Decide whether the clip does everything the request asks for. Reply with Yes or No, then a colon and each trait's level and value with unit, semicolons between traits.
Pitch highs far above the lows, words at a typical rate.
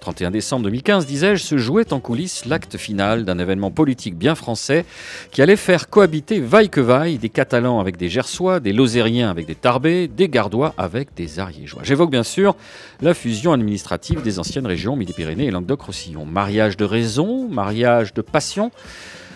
Yes: wide, 7.7 semitones; average, 170 wpm